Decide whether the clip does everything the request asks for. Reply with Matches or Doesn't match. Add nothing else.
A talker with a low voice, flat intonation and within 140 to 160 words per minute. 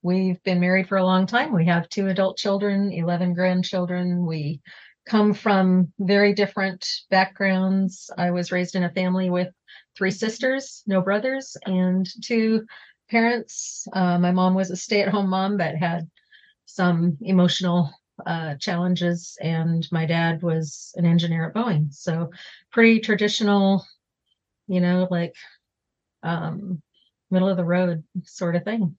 Doesn't match